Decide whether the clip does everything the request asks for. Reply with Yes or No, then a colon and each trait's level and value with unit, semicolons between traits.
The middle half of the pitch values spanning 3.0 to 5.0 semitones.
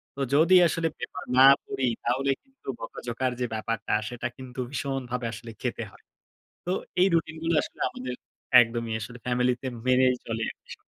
No: narrow, 2.6 semitones